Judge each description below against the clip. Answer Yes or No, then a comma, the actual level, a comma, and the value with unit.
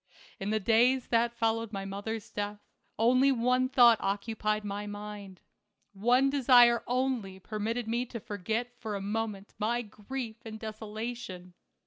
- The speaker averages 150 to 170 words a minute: No, average, 140 wpm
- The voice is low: No, high, 225 Hz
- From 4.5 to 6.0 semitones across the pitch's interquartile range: No, average, 2.7 semitones